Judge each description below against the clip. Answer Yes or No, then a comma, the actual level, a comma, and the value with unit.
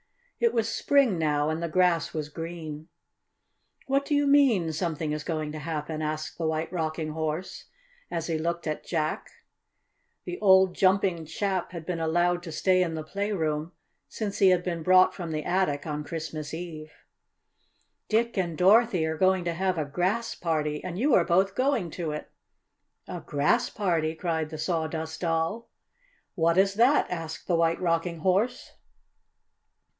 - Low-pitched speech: No, medium, 170 Hz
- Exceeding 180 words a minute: No, average, 160 wpm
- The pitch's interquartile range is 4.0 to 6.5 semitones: No, average, 3.2 semitones